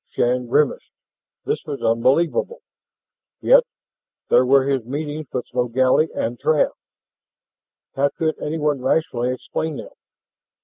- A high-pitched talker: No, medium, 140 Hz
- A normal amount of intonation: Yes, average, 3.6 semitones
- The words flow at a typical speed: No, slow, 115 wpm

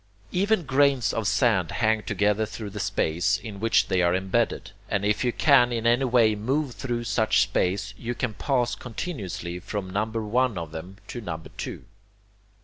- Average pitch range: Yes, average, 3.8 semitones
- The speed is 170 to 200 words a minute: Yes, average, 175 wpm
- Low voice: Yes, low, 110 Hz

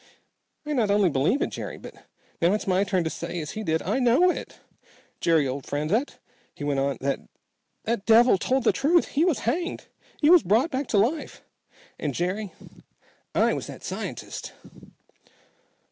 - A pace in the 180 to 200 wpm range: No, average, 170 wpm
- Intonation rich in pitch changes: Yes, wide, 8.3 semitones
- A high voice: Yes, high, 210 Hz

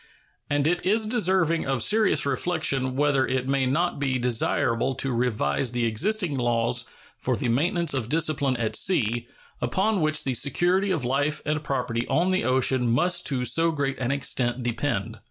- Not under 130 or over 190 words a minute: Yes, average, 170 wpm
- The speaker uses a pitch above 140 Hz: No, low, 135 Hz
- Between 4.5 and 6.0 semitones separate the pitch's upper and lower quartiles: Yes, average, 5.2 semitones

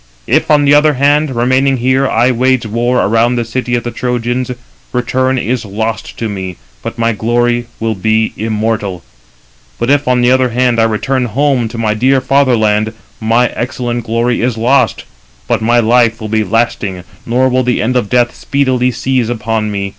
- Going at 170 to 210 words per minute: Yes, average, 185 wpm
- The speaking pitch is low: Yes, low, 120 Hz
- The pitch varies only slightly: Yes, narrow, 2.3 semitones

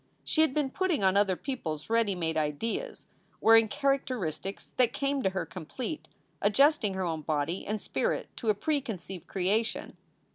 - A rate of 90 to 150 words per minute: No, average, 160 wpm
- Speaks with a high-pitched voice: Yes, high, 210 Hz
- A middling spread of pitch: No, wide, 6.8 semitones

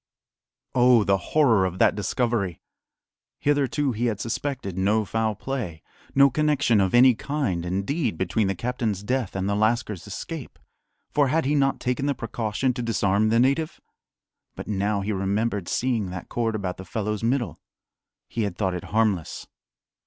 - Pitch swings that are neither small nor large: Yes, average, 4.6 semitones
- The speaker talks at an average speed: Yes, average, 160 wpm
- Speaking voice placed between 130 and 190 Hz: No, low, 110 Hz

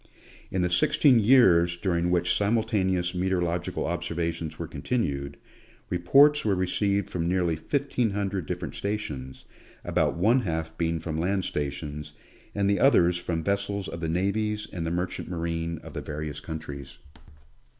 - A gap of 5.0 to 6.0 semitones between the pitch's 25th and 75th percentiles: No, average, 3.5 semitones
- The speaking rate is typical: Yes, average, 150 wpm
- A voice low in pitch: Yes, very low, 90 Hz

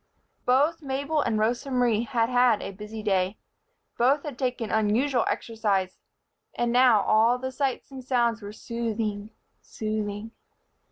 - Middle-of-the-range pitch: No, high, 235 Hz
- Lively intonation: No, average, 3.1 semitones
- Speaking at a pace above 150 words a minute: No, slow, 135 wpm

